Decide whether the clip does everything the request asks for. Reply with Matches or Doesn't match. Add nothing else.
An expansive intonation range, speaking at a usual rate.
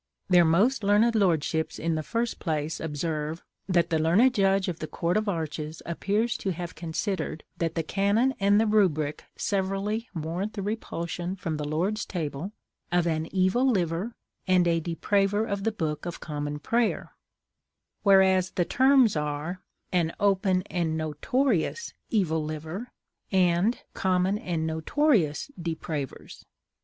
Doesn't match